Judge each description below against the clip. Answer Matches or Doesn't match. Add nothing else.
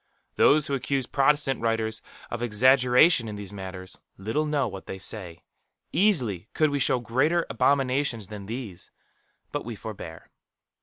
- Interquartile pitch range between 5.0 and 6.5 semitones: Matches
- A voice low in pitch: Matches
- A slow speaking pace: Doesn't match